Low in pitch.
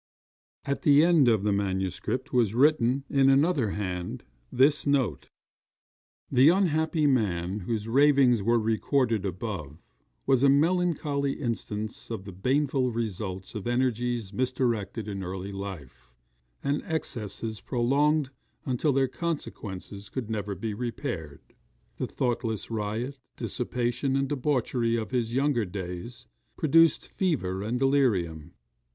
Yes: low, 120 Hz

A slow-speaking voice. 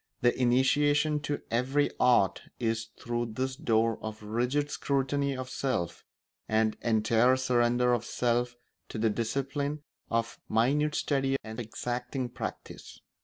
Yes: slow, 125 wpm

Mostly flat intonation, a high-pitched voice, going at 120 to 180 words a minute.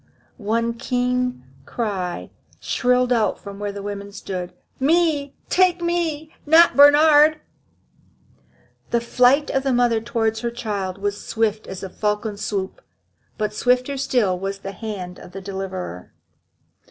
No: average, 5.1 semitones; high, 230 Hz; slow, 135 wpm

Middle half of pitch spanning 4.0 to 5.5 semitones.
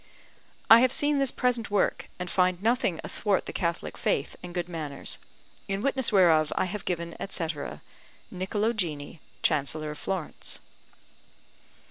Yes: average, 4.8 semitones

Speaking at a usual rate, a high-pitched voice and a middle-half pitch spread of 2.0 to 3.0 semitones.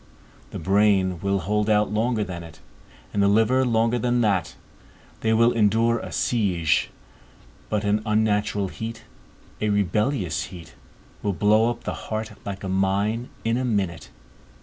No: average, 150 wpm; low, 105 Hz; narrow, 2.5 semitones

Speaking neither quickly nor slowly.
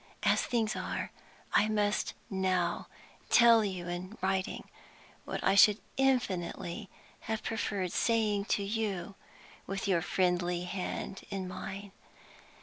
No: slow, 120 wpm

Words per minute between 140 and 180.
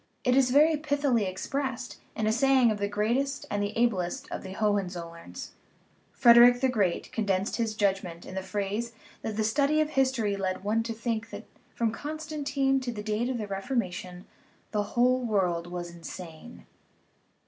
Yes: average, 175 wpm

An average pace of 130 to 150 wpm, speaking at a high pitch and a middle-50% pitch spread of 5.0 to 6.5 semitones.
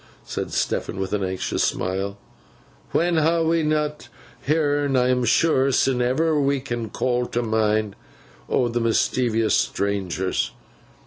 No: slow, 135 wpm; low, 125 Hz; wide, 5.5 semitones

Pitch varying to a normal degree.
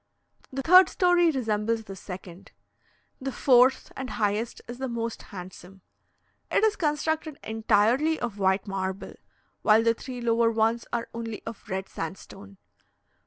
Yes: average, 4.6 semitones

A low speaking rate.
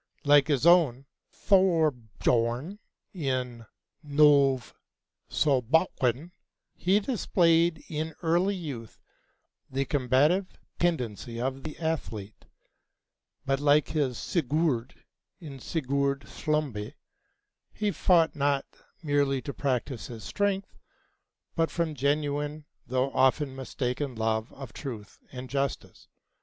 Yes: slow, 100 wpm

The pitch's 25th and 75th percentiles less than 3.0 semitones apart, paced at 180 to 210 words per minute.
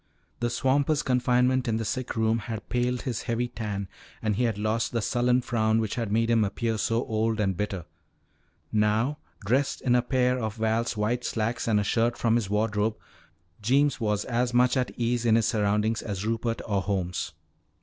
Yes: narrow, 2.4 semitones; average, 190 wpm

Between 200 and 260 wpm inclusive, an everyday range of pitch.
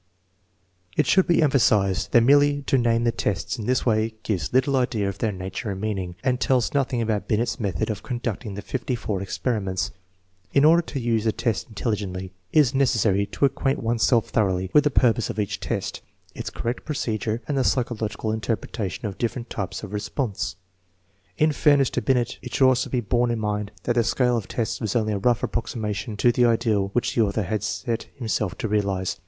Yes: fast, 205 wpm; average, 3.4 semitones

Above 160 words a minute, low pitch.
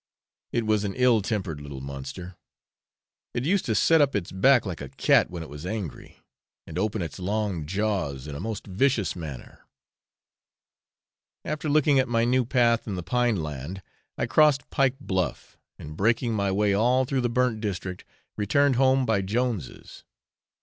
Yes: average, 170 wpm; low, 105 Hz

